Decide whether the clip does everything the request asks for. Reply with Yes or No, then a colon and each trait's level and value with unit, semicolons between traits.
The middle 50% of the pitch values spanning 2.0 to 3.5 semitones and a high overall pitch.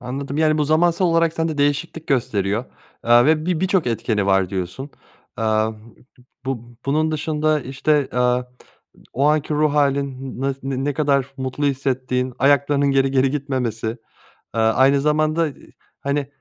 No: average, 3.1 semitones; medium, 140 Hz